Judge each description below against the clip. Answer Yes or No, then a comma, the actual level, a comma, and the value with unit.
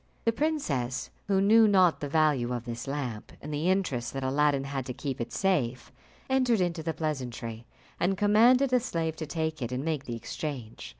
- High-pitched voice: No, medium, 150 Hz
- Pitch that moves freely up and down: Yes, wide, 7.0 semitones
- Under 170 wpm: No, average, 190 wpm